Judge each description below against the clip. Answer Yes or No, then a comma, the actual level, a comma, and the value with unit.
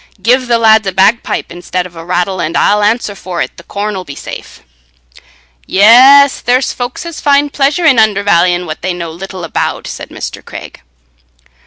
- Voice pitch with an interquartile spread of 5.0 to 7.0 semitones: Yes, wide, 5.6 semitones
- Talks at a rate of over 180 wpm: Yes, average, 190 wpm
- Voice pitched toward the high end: Yes, high, 205 Hz